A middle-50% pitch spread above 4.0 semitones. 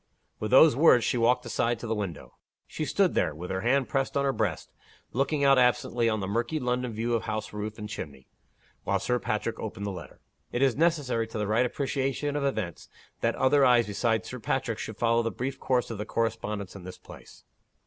No: average, 3.7 semitones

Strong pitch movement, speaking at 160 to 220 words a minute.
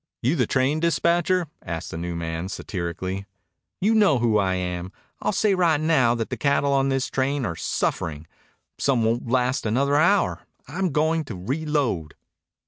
Yes: wide, 8.7 semitones; average, 165 wpm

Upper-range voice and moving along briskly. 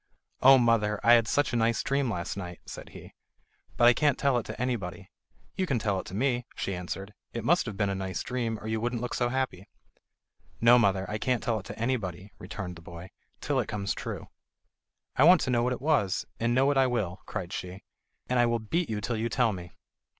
No: low, 115 Hz; fast, 230 wpm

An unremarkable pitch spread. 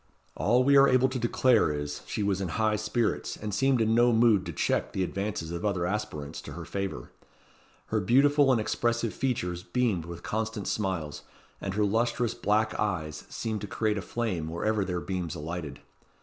Yes: average, 5.0 semitones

